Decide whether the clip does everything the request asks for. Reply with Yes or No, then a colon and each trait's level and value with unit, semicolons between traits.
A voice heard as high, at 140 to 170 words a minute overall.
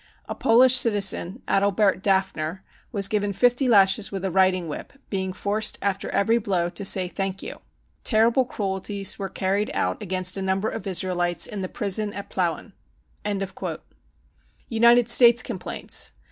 Yes: high, 195 Hz; average, 150 wpm